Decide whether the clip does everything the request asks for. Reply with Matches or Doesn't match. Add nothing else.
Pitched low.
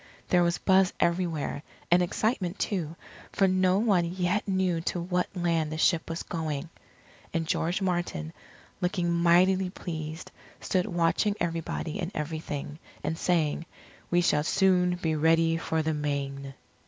Doesn't match